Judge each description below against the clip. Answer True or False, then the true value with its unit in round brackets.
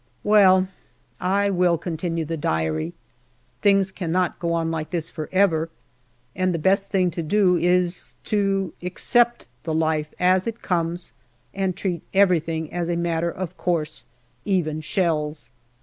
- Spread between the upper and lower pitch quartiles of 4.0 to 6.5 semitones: False (2.6 semitones)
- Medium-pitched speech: True (175 Hz)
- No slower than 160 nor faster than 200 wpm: False (145 wpm)